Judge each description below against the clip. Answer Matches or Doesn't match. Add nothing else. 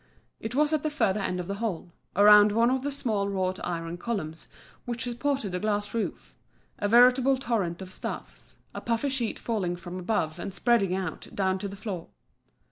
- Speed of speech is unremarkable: Matches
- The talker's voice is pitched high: Matches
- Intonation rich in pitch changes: Doesn't match